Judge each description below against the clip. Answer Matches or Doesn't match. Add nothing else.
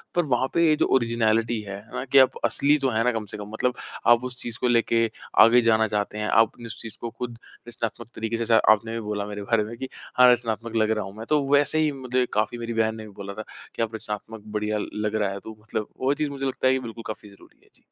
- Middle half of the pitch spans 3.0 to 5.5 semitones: Doesn't match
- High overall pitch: Doesn't match